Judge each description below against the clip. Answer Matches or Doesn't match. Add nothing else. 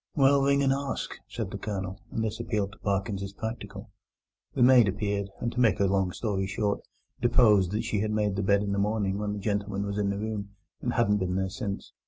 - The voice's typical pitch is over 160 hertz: Doesn't match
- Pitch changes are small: Matches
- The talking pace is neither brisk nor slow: Doesn't match